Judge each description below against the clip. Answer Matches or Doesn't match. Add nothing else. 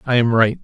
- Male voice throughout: Matches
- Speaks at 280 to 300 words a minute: Matches